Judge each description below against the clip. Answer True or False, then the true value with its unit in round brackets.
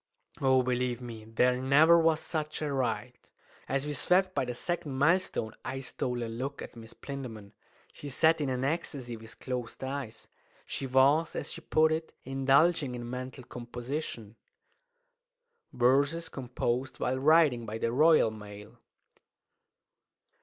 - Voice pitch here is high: False (130 Hz)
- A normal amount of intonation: True (3.7 semitones)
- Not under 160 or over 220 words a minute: False (145 wpm)